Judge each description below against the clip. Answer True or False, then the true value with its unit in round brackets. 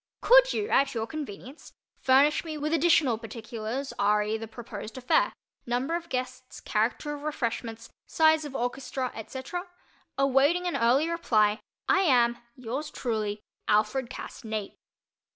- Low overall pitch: False (255 Hz)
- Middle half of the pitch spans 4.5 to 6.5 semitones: True (5.1 semitones)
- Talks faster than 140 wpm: False (135 wpm)